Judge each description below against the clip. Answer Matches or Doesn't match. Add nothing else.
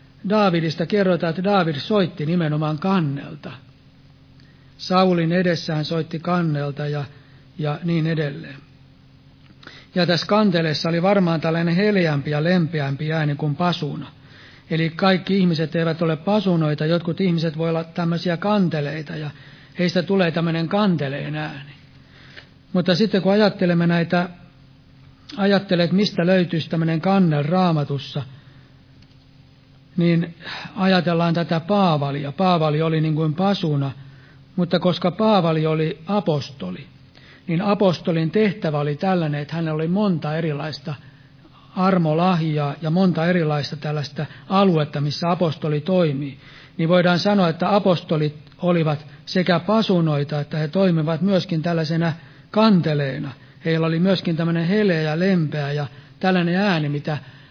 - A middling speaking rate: Matches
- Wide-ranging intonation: Doesn't match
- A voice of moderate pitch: Matches